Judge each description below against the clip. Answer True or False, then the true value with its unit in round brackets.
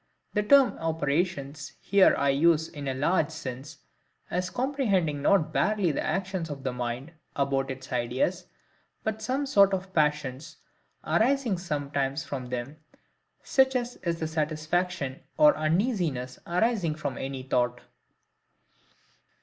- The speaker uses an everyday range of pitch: False (5.7 semitones)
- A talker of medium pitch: True (160 Hz)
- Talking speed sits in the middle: False (130 wpm)